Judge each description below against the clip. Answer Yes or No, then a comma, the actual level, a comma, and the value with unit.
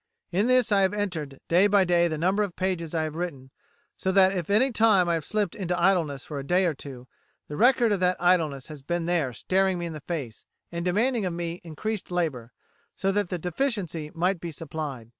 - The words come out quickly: Yes, fast, 225 wpm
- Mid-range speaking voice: Yes, medium, 175 Hz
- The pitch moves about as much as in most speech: Yes, average, 3.6 semitones